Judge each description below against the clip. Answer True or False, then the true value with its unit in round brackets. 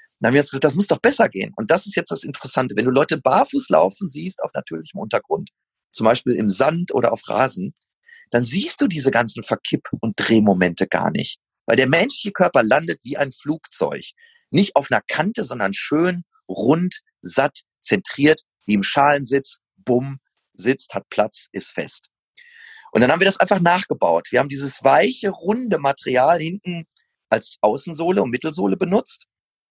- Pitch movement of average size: False (7.9 semitones)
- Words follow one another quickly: False (175 wpm)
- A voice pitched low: False (155 Hz)